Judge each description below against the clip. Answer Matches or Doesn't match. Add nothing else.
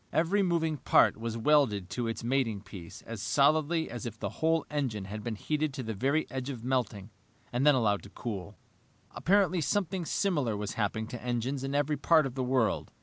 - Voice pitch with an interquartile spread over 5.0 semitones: Matches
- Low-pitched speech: Matches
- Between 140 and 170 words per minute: Doesn't match